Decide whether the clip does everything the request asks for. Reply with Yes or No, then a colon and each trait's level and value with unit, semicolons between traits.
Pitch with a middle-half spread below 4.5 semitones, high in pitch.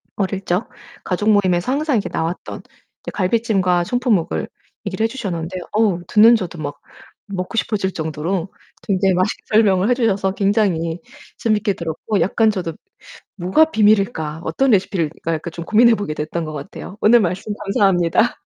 Yes: average, 3.9 semitones; high, 195 Hz